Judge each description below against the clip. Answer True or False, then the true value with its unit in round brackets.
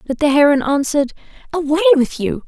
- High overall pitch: True (295 Hz)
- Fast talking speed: False (170 wpm)